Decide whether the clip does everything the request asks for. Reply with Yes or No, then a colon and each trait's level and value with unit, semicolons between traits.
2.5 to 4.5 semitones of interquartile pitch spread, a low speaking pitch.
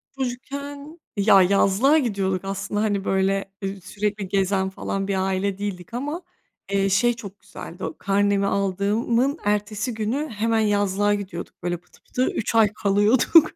No: average, 2.9 semitones; high, 205 Hz